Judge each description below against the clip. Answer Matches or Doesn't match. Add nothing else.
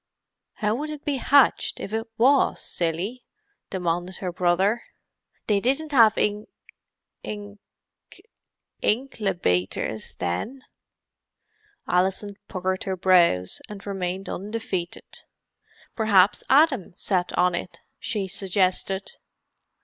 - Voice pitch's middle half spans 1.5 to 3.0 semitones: Doesn't match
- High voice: Matches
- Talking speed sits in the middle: Doesn't match